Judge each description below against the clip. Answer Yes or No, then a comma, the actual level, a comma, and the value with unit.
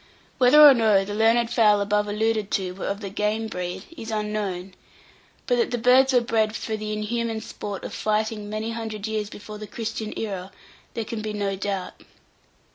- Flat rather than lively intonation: Yes, narrow, 1.6 semitones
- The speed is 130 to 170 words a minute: No, average, 190 wpm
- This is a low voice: No, high, 215 Hz